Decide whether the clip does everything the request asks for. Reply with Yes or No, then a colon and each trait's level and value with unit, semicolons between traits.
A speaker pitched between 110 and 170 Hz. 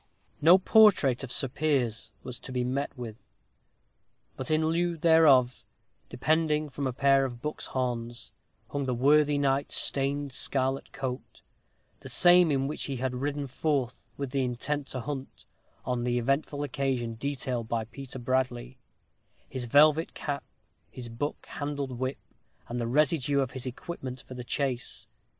Yes: low, 135 Hz